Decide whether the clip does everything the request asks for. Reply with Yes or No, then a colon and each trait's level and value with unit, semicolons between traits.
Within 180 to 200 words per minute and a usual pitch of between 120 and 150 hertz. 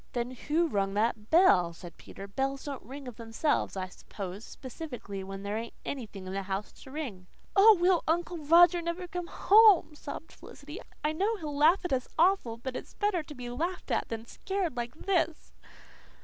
No: average, 190 wpm; very high, 280 Hz